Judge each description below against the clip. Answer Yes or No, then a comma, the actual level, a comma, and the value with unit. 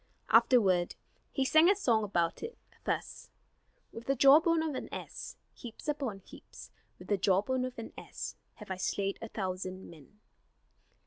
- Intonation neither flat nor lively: No, wide, 6.1 semitones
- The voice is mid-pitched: No, high, 225 Hz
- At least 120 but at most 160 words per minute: Yes, average, 155 wpm